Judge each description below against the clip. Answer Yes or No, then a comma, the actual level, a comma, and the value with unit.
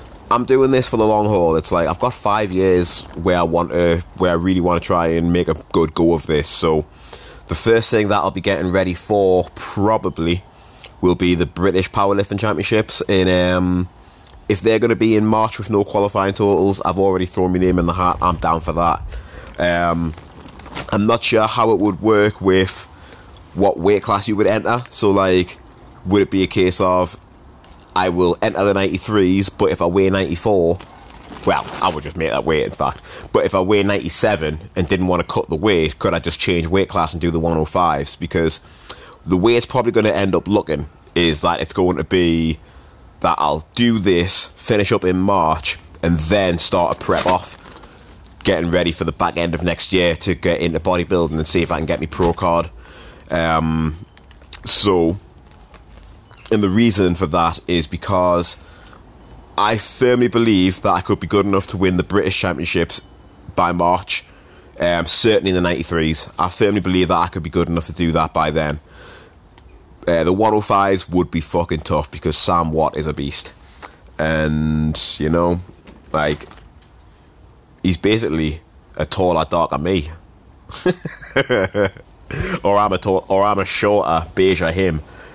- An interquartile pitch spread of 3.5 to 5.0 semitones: No, average, 3.0 semitones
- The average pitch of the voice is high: No, very low, 90 Hz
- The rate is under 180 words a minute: No, average, 185 wpm